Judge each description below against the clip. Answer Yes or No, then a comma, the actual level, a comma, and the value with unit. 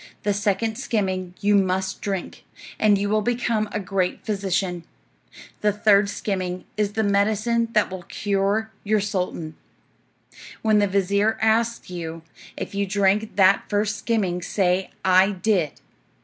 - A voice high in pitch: Yes, high, 200 Hz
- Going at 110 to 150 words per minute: Yes, average, 140 wpm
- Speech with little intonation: Yes, narrow, 2.2 semitones